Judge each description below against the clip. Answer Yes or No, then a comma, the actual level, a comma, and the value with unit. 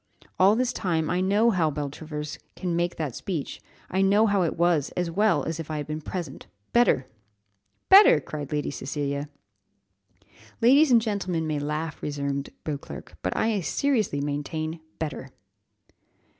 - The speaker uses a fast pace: No, average, 155 wpm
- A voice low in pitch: No, medium, 160 Hz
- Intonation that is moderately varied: Yes, average, 4.9 semitones